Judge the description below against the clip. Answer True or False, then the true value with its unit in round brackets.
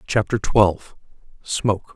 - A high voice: False (100 Hz)